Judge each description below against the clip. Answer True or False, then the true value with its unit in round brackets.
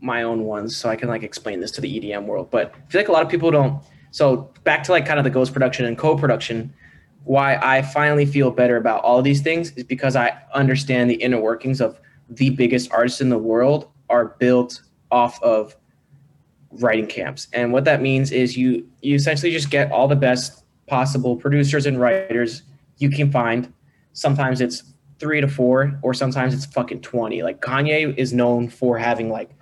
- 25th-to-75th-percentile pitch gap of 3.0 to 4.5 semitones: False (2.6 semitones)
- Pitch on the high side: False (130 Hz)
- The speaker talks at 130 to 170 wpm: False (200 wpm)